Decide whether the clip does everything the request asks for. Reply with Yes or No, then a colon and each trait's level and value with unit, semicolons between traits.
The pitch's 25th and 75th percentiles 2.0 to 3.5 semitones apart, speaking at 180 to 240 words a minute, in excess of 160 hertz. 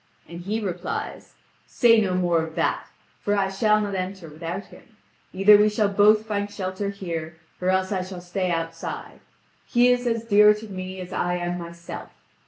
Yes: average, 3.0 semitones; average, 185 wpm; high, 190 Hz